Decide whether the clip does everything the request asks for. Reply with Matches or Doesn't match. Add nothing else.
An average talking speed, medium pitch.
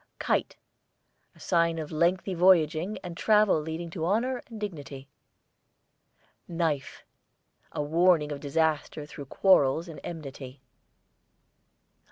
Doesn't match